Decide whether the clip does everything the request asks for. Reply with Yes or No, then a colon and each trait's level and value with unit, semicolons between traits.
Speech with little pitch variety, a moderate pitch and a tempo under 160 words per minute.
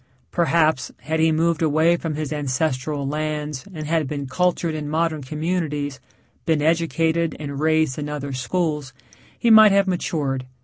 Yes: narrow, 2.3 semitones; medium, 155 Hz; average, 150 wpm